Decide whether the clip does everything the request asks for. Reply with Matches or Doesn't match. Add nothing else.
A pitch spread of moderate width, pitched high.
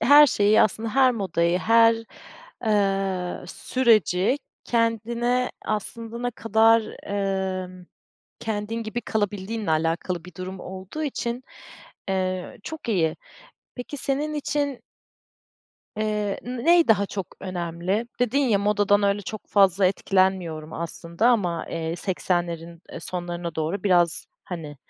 Matches